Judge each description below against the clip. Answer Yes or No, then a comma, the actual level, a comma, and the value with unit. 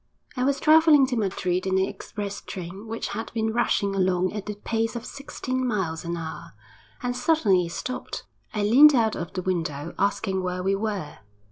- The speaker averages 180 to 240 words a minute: Yes, average, 190 wpm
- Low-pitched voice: No, high, 205 Hz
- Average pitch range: Yes, average, 4.6 semitones